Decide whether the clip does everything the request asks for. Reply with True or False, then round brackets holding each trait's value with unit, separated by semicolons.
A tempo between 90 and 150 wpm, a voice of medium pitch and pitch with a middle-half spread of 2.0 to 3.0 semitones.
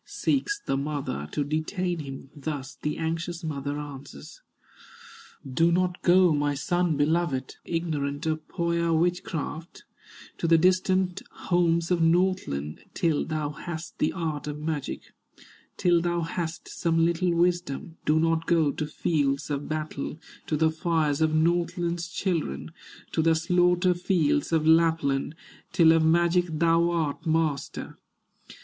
True (135 wpm; 165 Hz; 2.5 semitones)